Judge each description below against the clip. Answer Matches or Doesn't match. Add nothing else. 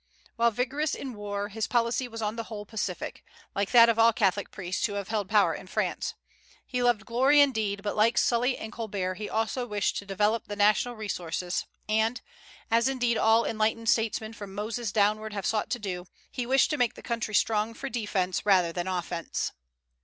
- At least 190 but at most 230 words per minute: Matches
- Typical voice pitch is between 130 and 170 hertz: Doesn't match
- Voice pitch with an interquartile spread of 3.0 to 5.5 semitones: Doesn't match